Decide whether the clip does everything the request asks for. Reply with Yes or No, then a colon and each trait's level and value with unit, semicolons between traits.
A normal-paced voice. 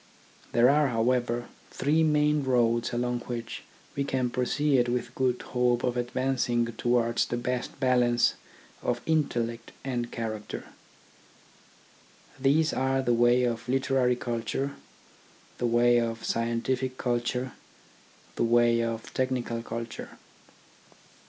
No: slow, 120 wpm